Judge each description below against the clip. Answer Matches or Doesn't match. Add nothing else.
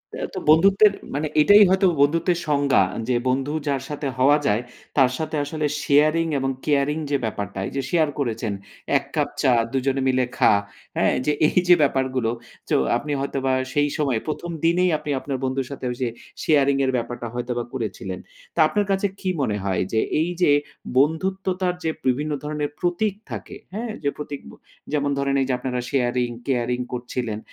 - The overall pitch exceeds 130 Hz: Matches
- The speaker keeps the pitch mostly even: Doesn't match